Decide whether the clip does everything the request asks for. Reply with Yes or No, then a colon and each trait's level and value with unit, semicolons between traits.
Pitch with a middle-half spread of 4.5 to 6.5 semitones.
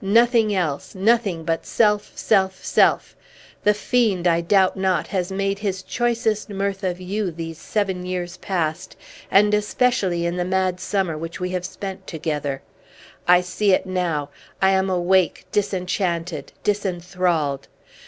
No: narrow, 2.5 semitones